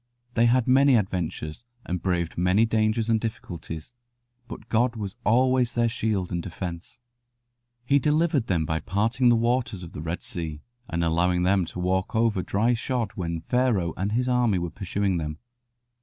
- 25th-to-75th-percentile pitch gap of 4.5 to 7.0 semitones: Yes, average, 5.2 semitones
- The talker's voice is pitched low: Yes, low, 100 Hz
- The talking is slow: No, average, 170 wpm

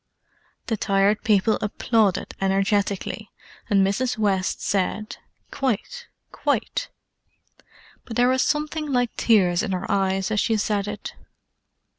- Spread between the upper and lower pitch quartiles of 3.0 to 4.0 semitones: Yes, average, 3.3 semitones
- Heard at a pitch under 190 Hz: No, high, 210 Hz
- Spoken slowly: Yes, slow, 115 wpm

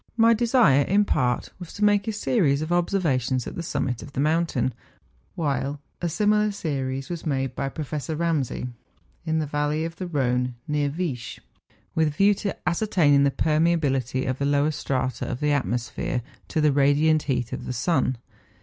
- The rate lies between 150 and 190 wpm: Yes, average, 180 wpm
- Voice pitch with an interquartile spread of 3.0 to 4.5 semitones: Yes, average, 4.2 semitones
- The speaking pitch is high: No, medium, 150 Hz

